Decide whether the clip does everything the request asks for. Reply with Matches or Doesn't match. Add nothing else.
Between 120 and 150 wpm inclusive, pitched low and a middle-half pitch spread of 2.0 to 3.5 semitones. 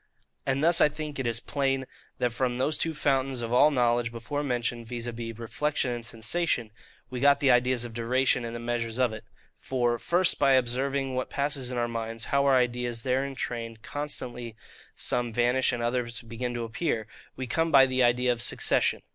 Doesn't match